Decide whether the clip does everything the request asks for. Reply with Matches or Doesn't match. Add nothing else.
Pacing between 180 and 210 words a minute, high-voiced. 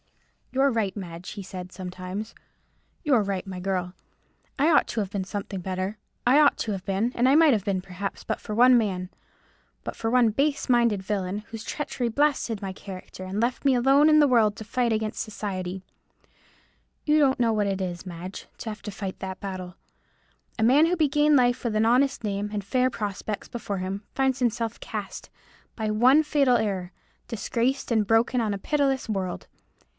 Matches